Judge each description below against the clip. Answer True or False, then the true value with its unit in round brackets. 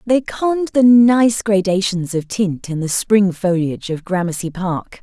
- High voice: True (195 Hz)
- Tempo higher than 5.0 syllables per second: False (4.3 syllables/s)